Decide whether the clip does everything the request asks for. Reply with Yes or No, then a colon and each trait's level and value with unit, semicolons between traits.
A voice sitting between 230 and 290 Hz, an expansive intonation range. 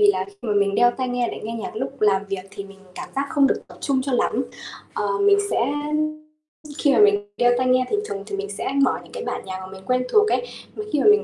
Yes: very high, 250 Hz; wide, 6.4 semitones